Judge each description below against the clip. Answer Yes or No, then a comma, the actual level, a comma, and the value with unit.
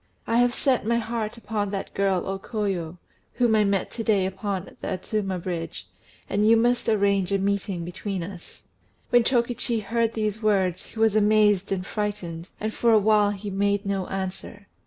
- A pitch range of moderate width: No, narrow, 2.3 semitones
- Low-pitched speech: No, high, 205 Hz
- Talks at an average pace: Yes, average, 180 wpm